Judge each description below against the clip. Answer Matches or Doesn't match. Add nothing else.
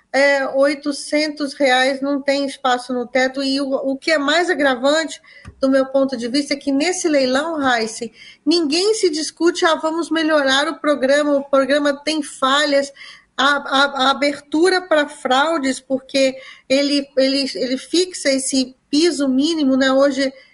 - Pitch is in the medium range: Doesn't match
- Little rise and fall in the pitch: Matches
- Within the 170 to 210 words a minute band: Doesn't match